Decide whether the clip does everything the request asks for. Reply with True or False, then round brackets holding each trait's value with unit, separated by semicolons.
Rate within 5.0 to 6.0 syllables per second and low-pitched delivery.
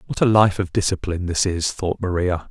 True (5.5 syllables/s; 90 Hz)